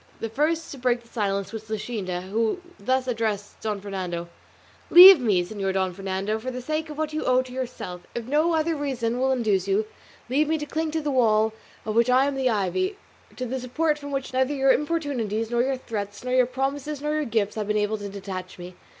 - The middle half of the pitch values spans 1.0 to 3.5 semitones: No, wide, 5.4 semitones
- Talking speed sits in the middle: No, fast, 220 wpm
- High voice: Yes, high, 245 Hz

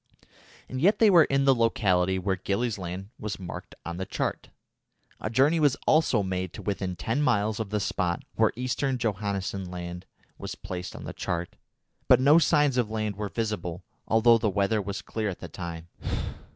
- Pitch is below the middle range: Yes, low, 105 Hz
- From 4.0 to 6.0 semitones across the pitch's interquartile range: Yes, average, 4.6 semitones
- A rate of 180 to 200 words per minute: Yes, average, 185 wpm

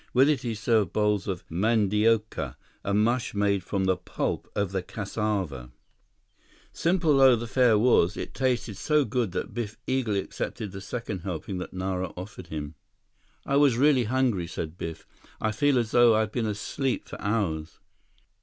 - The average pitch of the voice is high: No, low, 105 Hz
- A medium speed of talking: Yes, average, 170 wpm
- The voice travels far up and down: No, average, 4.3 semitones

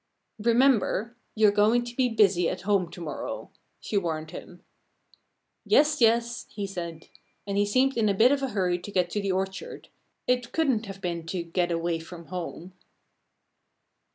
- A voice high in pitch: Yes, high, 200 Hz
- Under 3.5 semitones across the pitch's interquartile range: No, average, 4.9 semitones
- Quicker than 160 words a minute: Yes, average, 170 wpm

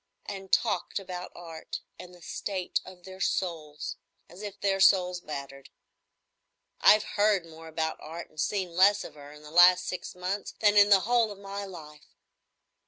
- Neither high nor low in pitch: Yes, medium, 180 Hz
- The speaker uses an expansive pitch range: No, average, 3.4 semitones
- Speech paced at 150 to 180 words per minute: Yes, average, 170 wpm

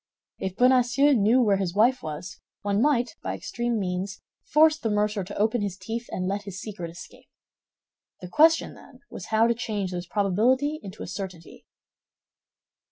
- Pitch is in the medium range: No, high, 210 Hz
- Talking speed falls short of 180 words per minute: Yes, average, 165 wpm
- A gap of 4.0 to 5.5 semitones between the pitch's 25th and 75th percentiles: Yes, average, 4.3 semitones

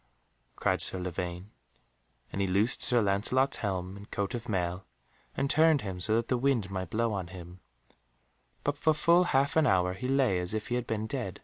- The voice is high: No, low, 105 Hz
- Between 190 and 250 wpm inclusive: Yes, average, 200 wpm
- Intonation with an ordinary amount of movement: No, wide, 5.7 semitones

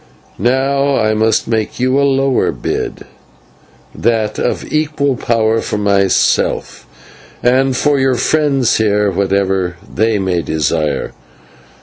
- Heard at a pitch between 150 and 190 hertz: No, low, 115 Hz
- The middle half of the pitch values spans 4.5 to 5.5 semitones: Yes, average, 5.1 semitones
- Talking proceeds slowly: Yes, slow, 115 wpm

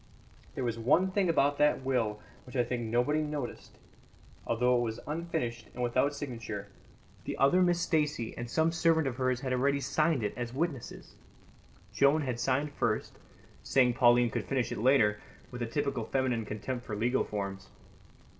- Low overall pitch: Yes, low, 130 Hz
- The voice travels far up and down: No, average, 3.6 semitones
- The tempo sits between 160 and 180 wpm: Yes, average, 170 wpm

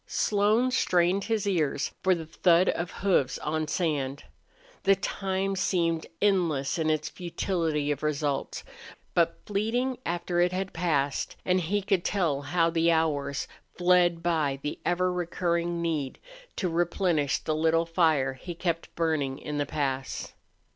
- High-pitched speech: No, medium, 170 Hz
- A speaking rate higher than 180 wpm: No, average, 145 wpm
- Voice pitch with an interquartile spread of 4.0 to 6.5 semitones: No, average, 3.2 semitones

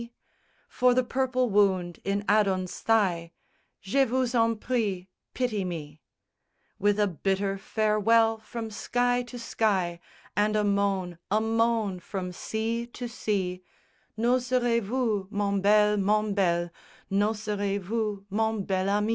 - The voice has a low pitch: No, high, 210 Hz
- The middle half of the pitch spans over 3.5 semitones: No, average, 2.8 semitones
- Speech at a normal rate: No, slow, 130 wpm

